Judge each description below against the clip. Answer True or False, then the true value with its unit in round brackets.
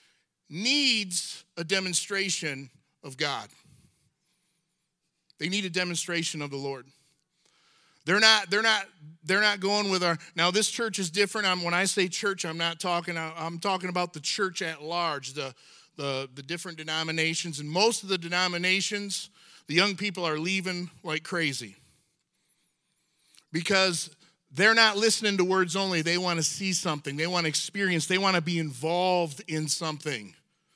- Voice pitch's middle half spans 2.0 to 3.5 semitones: True (3.0 semitones)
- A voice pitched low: False (175 Hz)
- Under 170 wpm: True (160 wpm)